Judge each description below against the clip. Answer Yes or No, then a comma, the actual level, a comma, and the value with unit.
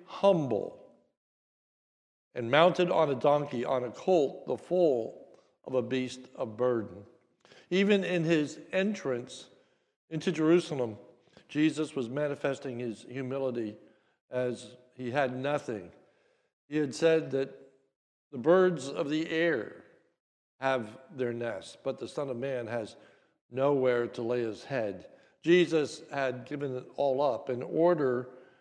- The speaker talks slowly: Yes, slow, 130 wpm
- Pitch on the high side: No, low, 135 Hz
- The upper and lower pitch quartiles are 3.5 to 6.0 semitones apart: Yes, average, 4.3 semitones